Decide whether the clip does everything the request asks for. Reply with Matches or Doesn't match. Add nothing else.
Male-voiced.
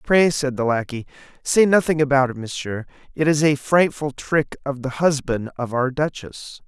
Matches